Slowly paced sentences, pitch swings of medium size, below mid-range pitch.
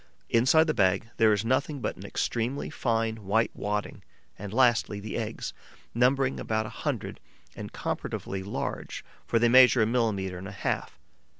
No: average, 165 wpm; average, 3.2 semitones; low, 115 Hz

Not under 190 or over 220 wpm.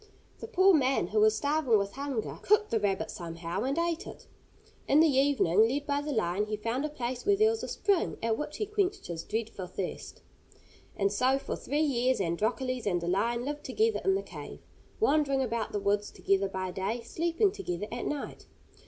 Yes: average, 200 wpm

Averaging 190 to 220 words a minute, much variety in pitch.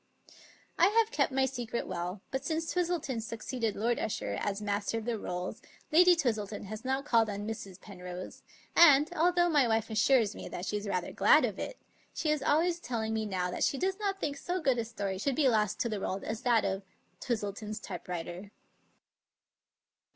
Yes: average, 200 wpm; wide, 6.0 semitones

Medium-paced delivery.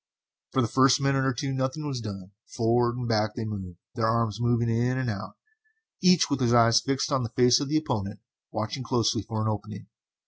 No: fast, 210 wpm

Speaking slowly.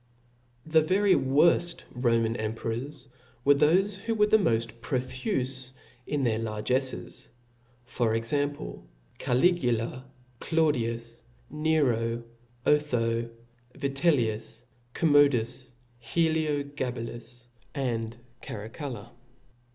Yes: slow, 80 wpm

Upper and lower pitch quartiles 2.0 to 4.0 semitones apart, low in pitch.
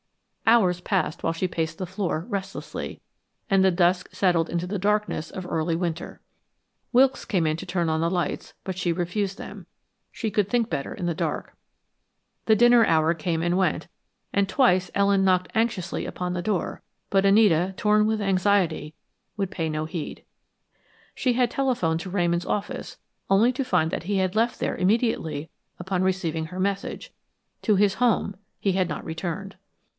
No: average, 3.1 semitones; medium, 185 Hz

